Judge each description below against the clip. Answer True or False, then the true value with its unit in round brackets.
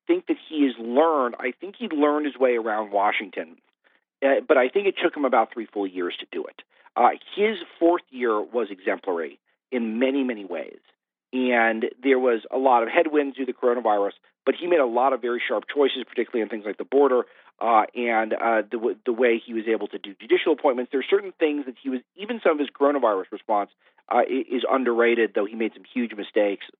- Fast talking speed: True (220 wpm)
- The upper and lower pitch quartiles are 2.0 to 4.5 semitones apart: False (4.9 semitones)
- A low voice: True (130 Hz)